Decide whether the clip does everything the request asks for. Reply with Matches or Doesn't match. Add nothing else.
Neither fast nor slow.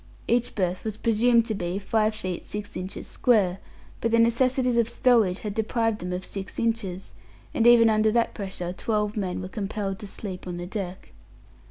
Matches